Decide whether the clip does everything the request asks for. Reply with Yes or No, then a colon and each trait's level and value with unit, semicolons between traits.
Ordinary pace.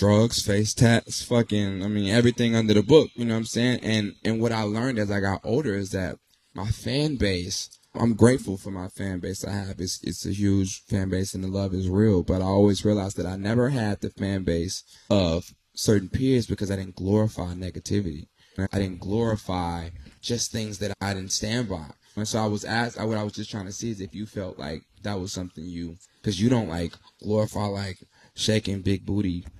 No: fast, 215 wpm